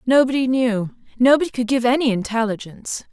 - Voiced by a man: No, female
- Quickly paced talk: No, slow, 135 wpm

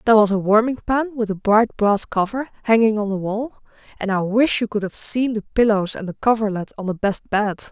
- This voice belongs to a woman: Yes, female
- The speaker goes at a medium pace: No, fast, 235 wpm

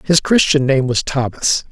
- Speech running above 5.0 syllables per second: No, 4.4 syllables/s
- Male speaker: Yes, male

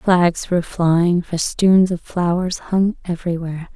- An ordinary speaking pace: No, slow, 130 wpm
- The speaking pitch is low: No, medium, 175 Hz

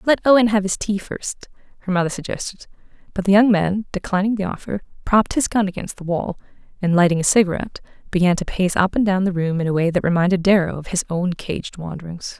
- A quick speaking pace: Yes, fast, 220 wpm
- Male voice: No, female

